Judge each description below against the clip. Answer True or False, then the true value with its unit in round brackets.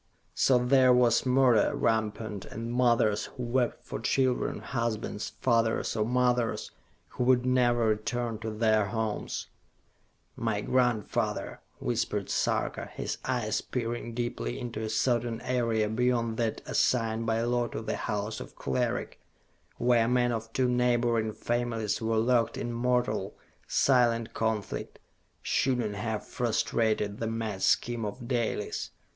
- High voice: False (115 Hz)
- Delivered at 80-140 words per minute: True (135 wpm)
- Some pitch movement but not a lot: False (1.8 semitones)